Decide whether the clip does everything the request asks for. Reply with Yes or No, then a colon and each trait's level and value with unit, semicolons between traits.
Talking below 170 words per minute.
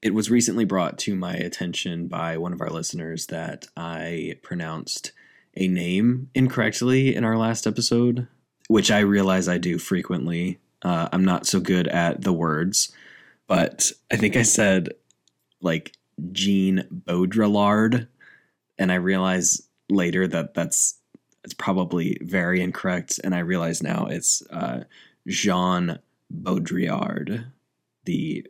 Yes: slow, 135 wpm